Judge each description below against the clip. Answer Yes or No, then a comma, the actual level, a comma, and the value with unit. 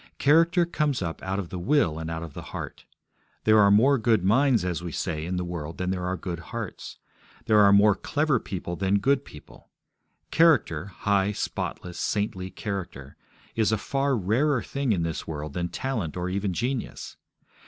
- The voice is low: Yes, low, 100 Hz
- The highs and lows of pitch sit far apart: Yes, wide, 6.0 semitones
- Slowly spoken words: No, average, 185 wpm